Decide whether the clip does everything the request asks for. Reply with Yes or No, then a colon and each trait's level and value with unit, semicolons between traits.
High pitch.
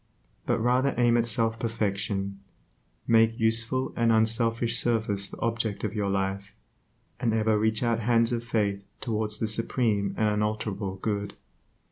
No: low, 110 Hz